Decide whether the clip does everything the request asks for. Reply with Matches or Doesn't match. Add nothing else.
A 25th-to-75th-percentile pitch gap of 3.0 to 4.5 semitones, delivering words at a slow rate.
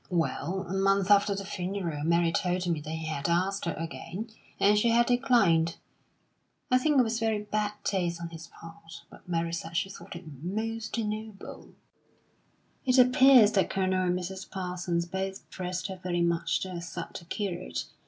Doesn't match